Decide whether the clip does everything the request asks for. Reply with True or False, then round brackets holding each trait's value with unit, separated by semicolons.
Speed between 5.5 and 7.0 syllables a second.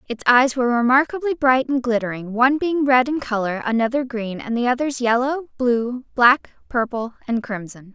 False (5.1 syllables/s)